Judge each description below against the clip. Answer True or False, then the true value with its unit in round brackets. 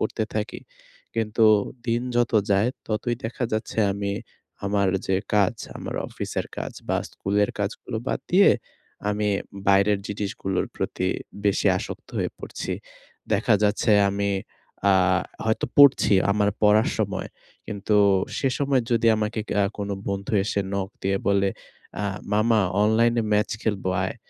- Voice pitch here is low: True (105 Hz)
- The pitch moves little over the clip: True (2.1 semitones)